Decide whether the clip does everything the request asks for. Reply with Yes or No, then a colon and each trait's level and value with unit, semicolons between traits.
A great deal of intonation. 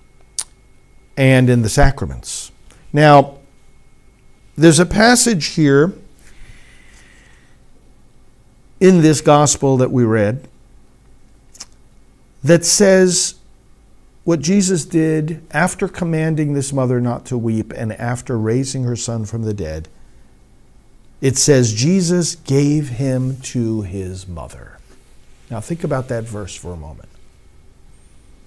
Yes: wide, 6.1 semitones